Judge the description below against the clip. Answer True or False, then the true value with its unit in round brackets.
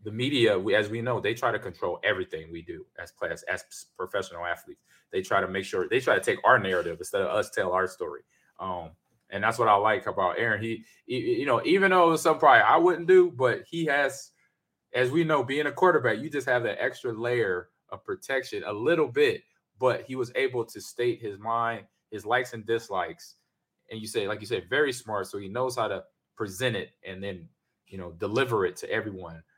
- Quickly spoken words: True (225 wpm)